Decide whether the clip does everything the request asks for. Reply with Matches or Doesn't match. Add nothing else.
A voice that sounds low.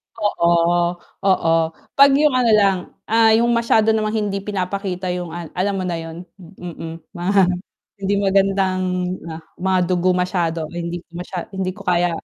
Doesn't match